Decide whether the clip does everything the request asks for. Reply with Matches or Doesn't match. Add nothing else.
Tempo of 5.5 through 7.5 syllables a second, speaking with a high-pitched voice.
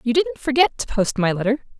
Matches